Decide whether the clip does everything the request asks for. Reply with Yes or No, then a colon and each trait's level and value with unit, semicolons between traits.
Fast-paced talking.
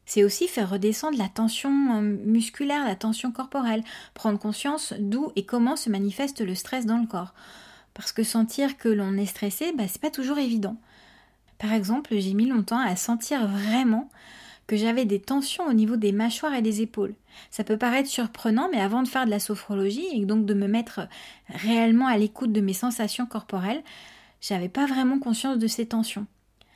No: average, 190 wpm